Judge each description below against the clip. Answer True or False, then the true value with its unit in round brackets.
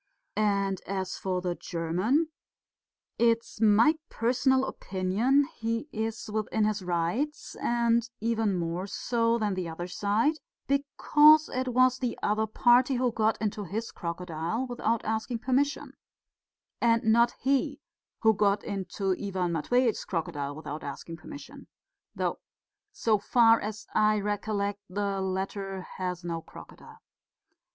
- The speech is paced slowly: True (130 wpm)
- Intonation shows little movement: False (4.1 semitones)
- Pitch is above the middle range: True (215 Hz)